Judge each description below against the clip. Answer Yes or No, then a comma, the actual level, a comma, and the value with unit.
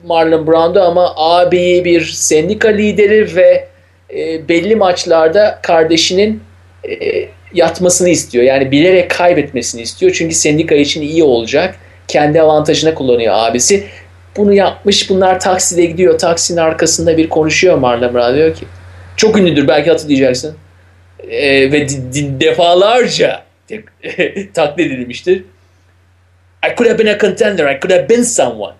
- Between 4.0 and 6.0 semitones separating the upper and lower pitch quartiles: Yes, wide, 5.5 semitones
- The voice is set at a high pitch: No, medium, 165 Hz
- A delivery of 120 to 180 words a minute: Yes, average, 130 wpm